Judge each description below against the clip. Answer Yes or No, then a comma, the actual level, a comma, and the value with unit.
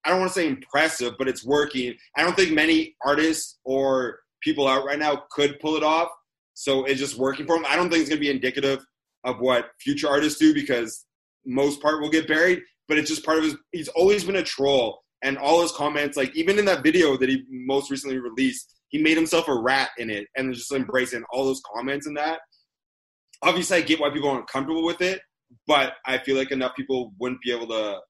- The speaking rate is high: Yes, fast, 230 wpm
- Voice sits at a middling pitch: Yes, medium, 145 Hz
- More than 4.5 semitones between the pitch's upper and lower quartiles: No, average, 3.3 semitones